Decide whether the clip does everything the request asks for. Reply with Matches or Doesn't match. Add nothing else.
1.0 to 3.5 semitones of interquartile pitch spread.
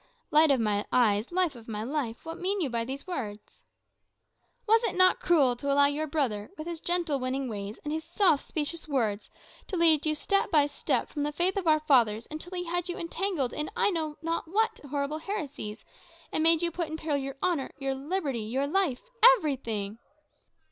Doesn't match